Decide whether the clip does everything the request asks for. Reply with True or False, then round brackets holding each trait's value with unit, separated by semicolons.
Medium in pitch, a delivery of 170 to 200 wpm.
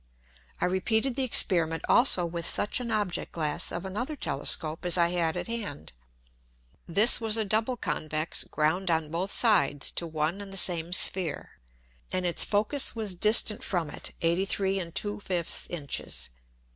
False (180 Hz; 155 wpm)